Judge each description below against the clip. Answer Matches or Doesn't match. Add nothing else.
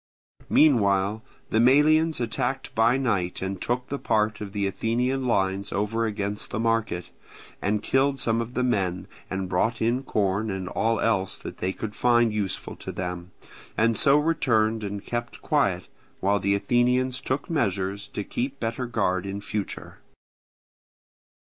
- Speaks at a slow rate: Doesn't match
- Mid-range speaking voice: Doesn't match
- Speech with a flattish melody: Doesn't match